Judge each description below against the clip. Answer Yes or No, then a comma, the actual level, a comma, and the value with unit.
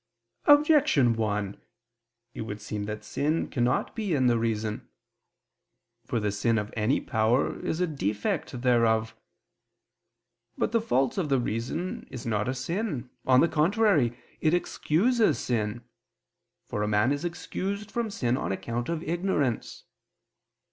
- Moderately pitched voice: No, low, 125 Hz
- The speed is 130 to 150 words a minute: Yes, average, 140 wpm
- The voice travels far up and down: Yes, wide, 7.4 semitones